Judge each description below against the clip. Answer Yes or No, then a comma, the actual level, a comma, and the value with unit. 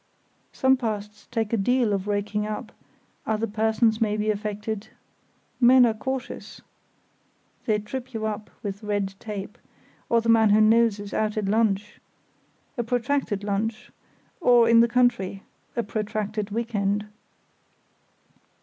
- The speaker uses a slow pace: Yes, slow, 130 wpm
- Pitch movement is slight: Yes, narrow, 2.0 semitones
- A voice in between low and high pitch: No, high, 215 Hz